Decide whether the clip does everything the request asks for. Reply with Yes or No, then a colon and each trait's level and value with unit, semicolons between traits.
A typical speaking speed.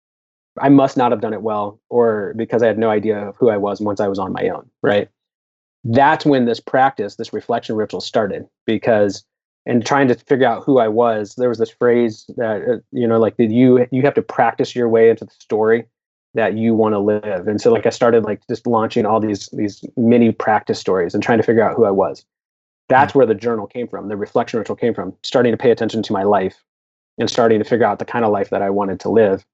No: fast, 240 wpm